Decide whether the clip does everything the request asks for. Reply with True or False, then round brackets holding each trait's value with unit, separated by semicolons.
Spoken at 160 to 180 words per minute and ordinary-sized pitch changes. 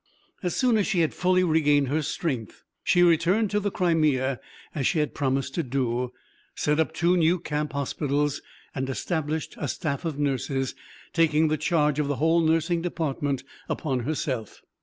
True (170 wpm; 3.3 semitones)